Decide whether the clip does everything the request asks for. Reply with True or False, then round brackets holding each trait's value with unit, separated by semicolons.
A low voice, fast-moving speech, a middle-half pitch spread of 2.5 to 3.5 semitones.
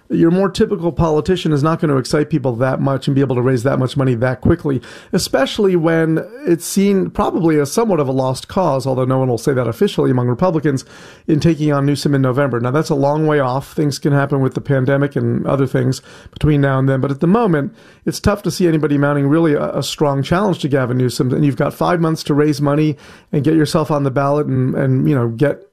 False (145 Hz; 245 wpm; 3.2 semitones)